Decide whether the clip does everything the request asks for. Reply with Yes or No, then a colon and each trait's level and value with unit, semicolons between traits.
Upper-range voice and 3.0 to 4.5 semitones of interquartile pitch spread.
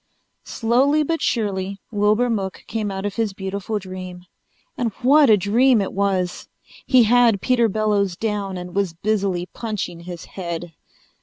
Yes: high, 205 Hz; average, 3.3 semitones